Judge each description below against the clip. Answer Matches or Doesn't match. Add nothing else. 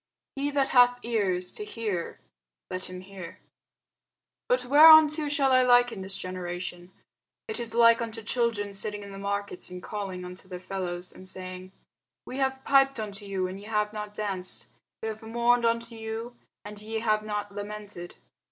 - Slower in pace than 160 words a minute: Doesn't match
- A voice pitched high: Matches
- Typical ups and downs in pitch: Matches